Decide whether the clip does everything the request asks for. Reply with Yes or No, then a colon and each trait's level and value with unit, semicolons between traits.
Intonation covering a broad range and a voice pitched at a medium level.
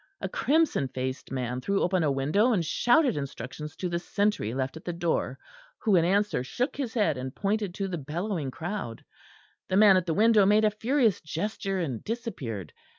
Yes: wide, 7.3 semitones; medium, 180 Hz